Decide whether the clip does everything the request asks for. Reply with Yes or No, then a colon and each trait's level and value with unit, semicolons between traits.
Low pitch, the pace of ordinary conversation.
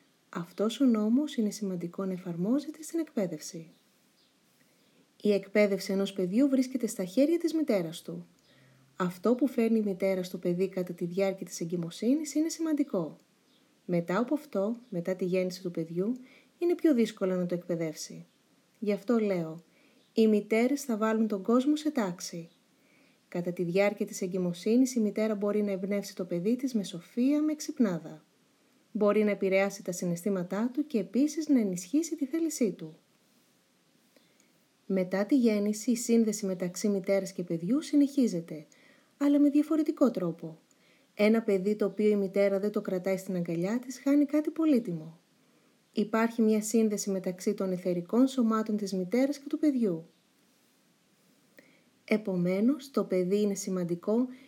No: high, 210 Hz; average, 150 wpm